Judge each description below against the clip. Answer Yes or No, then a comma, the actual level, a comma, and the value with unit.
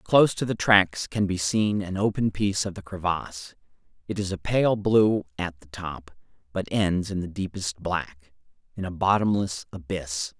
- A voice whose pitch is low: Yes, very low, 95 Hz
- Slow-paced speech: No, average, 180 wpm